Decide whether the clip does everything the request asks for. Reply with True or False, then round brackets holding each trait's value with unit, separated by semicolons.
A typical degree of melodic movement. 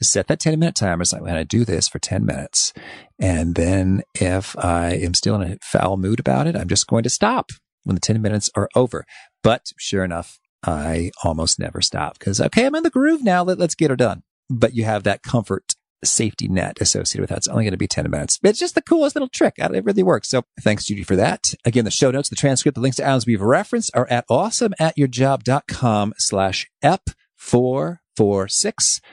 False (7.8 semitones)